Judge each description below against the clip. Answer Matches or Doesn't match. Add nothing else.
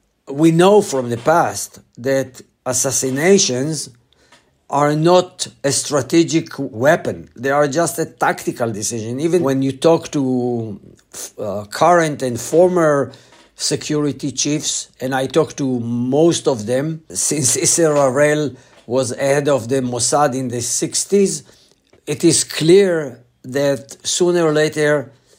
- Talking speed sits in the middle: Doesn't match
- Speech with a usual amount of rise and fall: Matches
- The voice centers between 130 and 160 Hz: Matches